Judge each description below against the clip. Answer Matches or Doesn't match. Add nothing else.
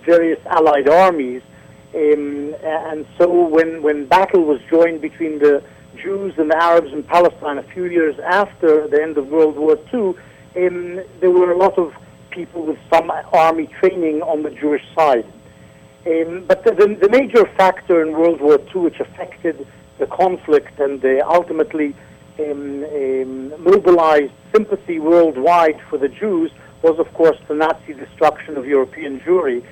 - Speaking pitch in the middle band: Matches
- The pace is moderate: Matches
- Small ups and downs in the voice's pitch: Doesn't match